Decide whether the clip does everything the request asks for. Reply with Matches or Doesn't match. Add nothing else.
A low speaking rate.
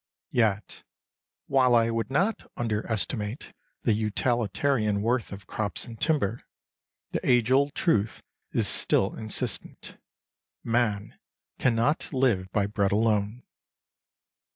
Matches